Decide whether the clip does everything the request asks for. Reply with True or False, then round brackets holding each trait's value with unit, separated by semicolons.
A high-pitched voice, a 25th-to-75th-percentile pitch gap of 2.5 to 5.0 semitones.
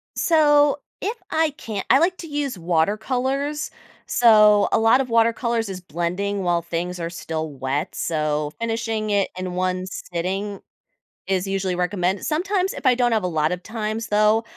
False (205 Hz; 5.4 semitones)